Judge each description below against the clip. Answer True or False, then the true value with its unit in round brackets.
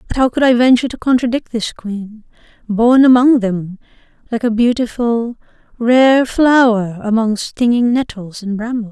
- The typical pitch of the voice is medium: False (235 Hz)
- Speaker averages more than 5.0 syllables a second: False (4.6 syllables/s)